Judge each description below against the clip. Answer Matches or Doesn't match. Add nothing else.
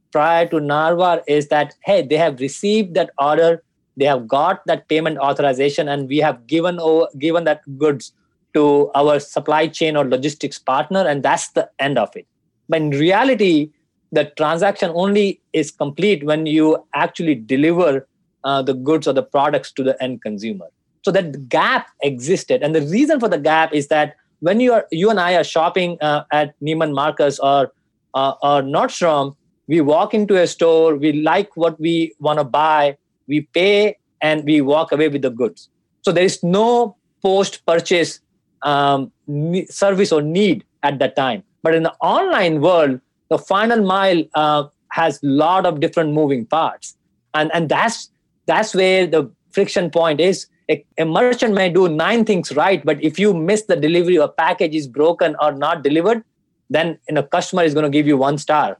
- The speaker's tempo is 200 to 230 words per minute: Doesn't match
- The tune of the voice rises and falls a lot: Doesn't match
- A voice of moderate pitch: Matches